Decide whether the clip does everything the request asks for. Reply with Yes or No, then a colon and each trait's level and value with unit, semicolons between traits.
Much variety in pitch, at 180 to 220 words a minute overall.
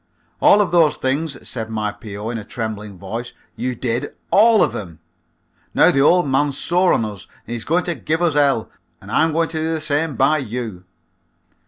Yes: wide, 6.4 semitones; average, 200 wpm